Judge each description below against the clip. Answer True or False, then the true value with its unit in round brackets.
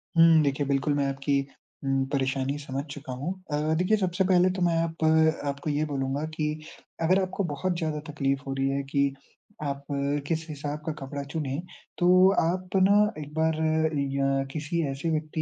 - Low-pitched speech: False (150 Hz)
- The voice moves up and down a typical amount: True (3.3 semitones)